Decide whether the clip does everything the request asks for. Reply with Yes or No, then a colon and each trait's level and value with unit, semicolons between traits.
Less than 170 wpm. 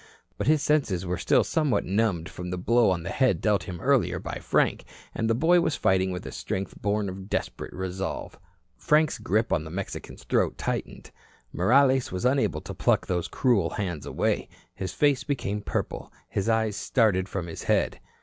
No: average, 185 wpm